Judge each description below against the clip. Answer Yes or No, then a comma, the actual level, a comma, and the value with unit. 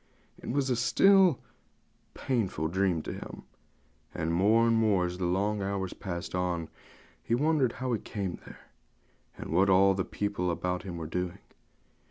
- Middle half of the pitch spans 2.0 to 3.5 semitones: No, average, 4.3 semitones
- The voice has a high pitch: No, very low, 95 Hz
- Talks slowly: No, average, 165 wpm